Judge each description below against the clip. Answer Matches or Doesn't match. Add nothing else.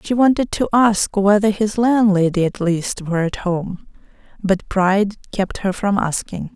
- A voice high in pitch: Matches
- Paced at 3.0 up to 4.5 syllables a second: Matches